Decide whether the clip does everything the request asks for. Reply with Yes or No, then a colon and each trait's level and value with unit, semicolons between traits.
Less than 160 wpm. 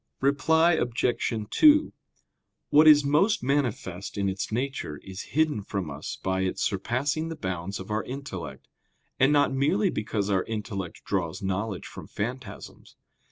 Yes: average, 145 wpm